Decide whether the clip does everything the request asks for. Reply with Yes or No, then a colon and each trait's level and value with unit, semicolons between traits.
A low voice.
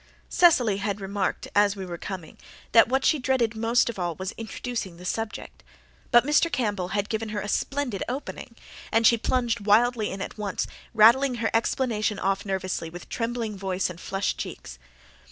No: high, 215 Hz